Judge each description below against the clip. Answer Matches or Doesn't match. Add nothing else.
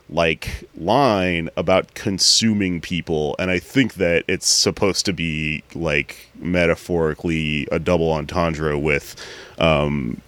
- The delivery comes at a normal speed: Doesn't match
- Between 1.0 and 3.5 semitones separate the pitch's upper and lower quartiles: Matches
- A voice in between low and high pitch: Doesn't match